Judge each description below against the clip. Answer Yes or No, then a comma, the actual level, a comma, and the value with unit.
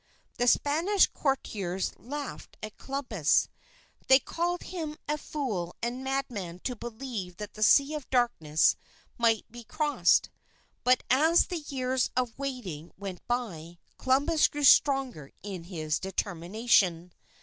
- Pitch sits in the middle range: No, high, 245 Hz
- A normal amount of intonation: No, wide, 6.7 semitones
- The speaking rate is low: Yes, slow, 125 wpm